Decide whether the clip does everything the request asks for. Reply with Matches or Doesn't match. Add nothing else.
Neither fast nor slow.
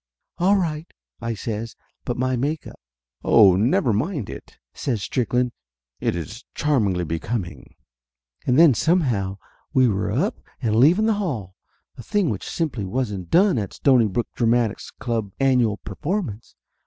Matches